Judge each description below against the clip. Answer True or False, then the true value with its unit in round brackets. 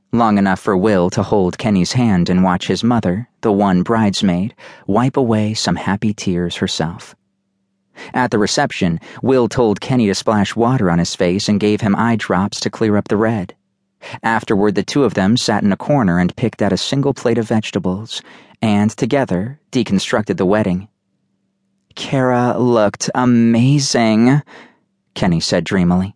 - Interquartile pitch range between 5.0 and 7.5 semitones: False (3.8 semitones)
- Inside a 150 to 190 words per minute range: True (165 wpm)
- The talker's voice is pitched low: True (105 Hz)